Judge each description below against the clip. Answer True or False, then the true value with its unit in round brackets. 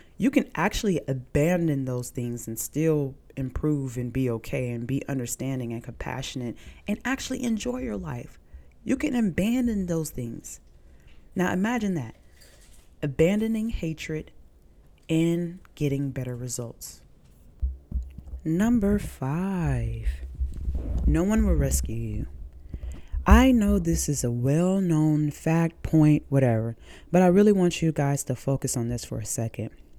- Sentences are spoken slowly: True (130 wpm)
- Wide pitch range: True (7.5 semitones)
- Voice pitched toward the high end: False (135 Hz)